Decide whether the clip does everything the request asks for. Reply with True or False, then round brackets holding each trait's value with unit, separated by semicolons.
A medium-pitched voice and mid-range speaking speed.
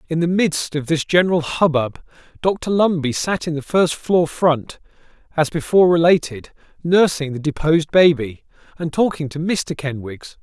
True (160 Hz; 155 wpm)